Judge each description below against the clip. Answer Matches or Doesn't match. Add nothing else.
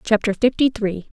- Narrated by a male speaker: Doesn't match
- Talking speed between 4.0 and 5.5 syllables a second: Matches